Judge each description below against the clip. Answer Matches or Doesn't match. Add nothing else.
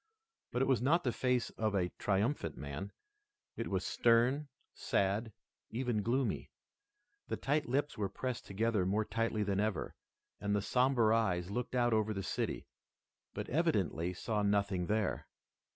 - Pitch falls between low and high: Doesn't match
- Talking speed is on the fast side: Doesn't match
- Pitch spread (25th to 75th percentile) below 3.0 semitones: Doesn't match